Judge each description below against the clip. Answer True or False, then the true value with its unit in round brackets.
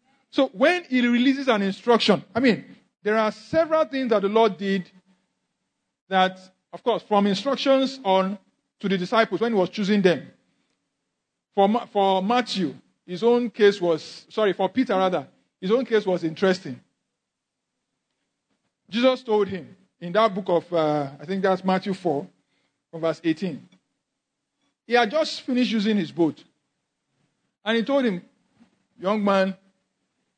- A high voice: True (200 Hz)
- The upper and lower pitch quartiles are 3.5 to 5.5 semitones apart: True (4.1 semitones)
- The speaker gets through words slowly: False (150 wpm)